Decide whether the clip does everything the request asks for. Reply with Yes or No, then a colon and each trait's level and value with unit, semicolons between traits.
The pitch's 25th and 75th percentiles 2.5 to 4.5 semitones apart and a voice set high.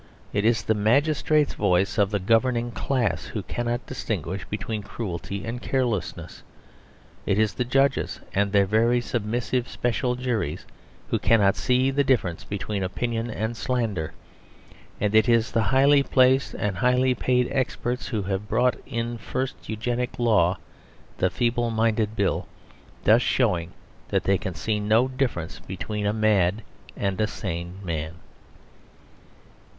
No: average, 3.7 semitones; low, 110 Hz